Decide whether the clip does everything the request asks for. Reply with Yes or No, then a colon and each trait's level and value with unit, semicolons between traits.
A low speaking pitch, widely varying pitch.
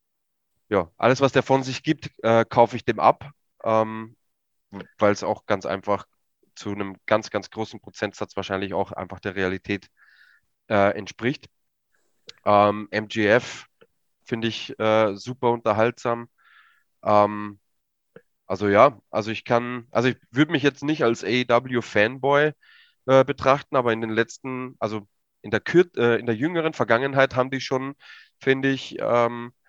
No: low, 115 Hz; average, 3.9 semitones